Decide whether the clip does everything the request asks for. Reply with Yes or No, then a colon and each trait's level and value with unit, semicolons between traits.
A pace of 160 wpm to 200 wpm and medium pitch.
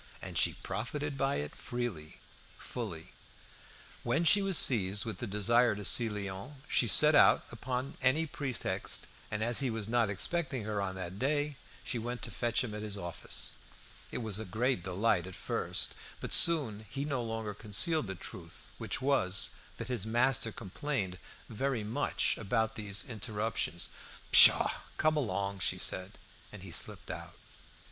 No: average, 165 wpm; low, 115 Hz